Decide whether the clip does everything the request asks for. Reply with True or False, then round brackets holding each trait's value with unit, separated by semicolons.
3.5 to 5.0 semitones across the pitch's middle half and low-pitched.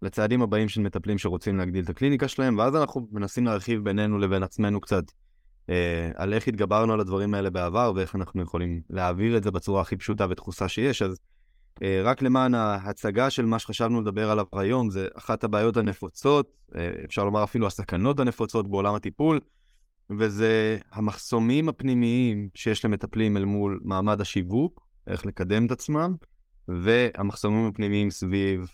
False (3.1 semitones; 105 Hz)